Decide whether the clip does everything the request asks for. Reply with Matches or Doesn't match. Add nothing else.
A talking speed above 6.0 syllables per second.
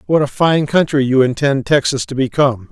Doesn't match